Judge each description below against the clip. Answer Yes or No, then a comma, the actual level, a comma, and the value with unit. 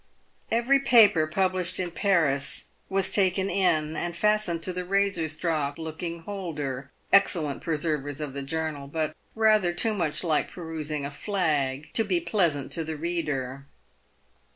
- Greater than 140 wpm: Yes, average, 150 wpm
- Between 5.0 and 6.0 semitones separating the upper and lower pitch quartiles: No, average, 4.0 semitones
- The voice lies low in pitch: No, medium, 165 Hz